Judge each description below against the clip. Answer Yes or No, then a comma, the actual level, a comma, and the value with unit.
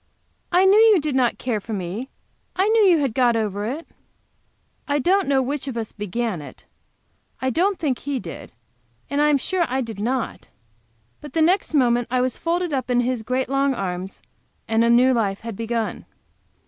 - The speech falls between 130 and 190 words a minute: No, average, 200 wpm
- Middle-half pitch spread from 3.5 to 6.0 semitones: Yes, average, 4.6 semitones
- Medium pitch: No, very high, 255 Hz